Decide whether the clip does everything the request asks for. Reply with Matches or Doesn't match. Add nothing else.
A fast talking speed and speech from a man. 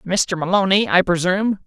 Doesn't match